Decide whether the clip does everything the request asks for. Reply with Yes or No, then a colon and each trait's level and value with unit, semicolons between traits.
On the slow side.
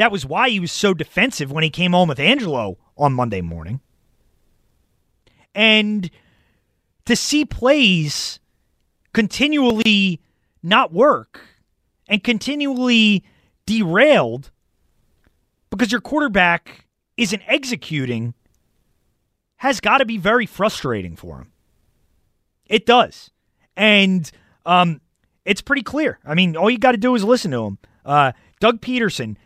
Yes: slow, 120 wpm